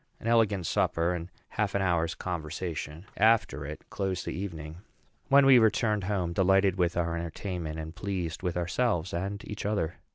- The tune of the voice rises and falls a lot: No, average, 3.4 semitones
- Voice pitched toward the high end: No, very low, 90 Hz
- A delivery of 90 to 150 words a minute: No, average, 165 wpm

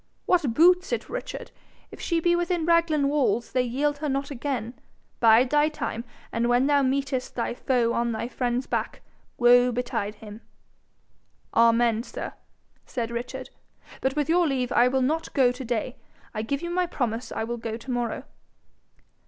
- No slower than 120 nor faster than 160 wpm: No, average, 170 wpm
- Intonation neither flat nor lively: Yes, average, 3.8 semitones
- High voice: Yes, very high, 255 Hz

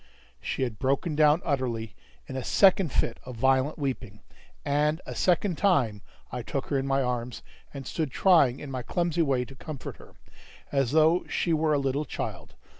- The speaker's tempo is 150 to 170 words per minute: No, average, 185 wpm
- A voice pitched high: No, medium, 140 Hz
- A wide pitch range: No, average, 3.7 semitones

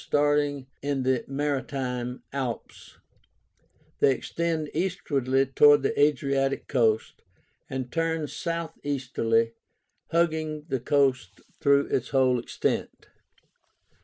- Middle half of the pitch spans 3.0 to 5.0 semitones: No, narrow, 2.5 semitones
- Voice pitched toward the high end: No, medium, 140 Hz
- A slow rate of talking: Yes, slow, 95 wpm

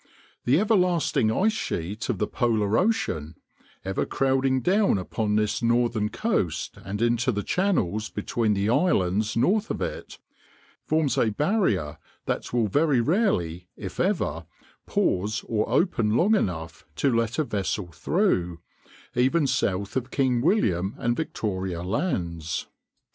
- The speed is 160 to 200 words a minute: No, slow, 135 wpm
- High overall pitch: No, low, 115 Hz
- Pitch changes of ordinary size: No, wide, 7.6 semitones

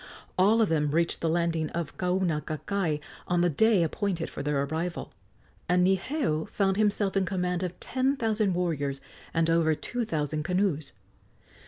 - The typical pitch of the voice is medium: Yes, medium, 175 Hz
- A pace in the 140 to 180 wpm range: Yes, average, 155 wpm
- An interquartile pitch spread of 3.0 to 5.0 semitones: Yes, average, 3.8 semitones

